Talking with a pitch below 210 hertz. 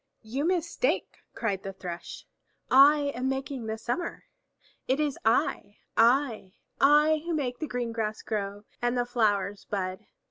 No: high, 245 Hz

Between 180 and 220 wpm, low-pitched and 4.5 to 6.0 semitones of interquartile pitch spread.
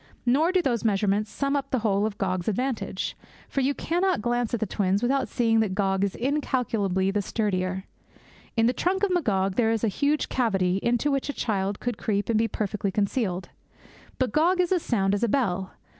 No: fast, 205 wpm; high, 225 Hz; average, 5.3 semitones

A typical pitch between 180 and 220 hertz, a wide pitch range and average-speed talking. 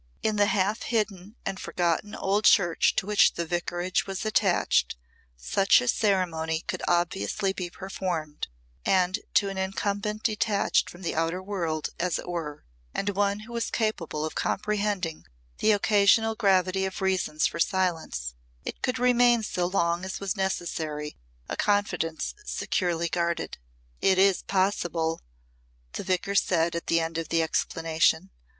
No: medium, 185 Hz; average, 3.3 semitones; average, 150 wpm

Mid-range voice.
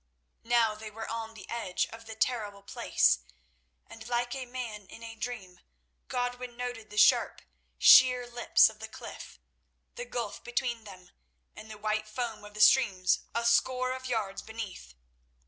No: high, 225 Hz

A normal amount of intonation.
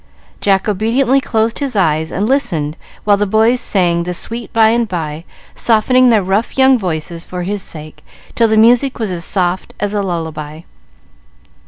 Yes: average, 4.9 semitones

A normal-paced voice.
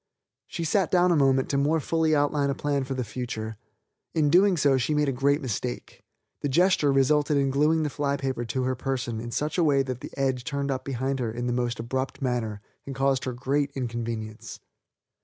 No: fast, 215 wpm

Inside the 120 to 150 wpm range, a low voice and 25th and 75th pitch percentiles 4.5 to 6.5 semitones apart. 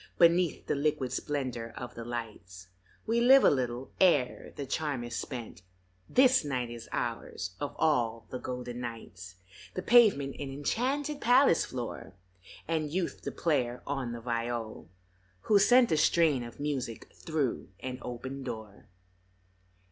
Yes: average, 145 wpm; low, 130 Hz; average, 5.2 semitones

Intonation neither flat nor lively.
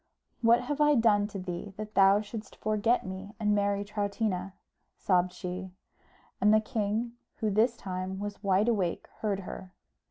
No: narrow, 2.3 semitones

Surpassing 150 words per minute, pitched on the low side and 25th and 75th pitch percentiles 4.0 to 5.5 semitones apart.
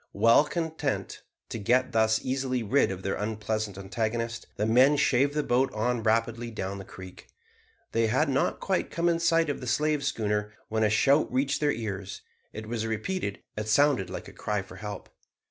Yes: average, 185 wpm; low, 115 Hz; average, 4.5 semitones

